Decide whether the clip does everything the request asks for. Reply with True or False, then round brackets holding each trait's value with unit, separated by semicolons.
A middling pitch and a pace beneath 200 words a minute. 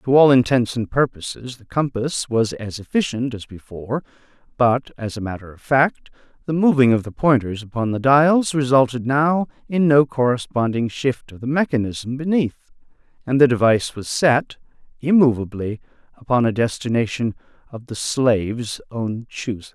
False (125 Hz; 150 wpm)